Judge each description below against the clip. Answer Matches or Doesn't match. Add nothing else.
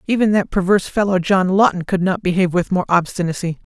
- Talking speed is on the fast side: Doesn't match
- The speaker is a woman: Matches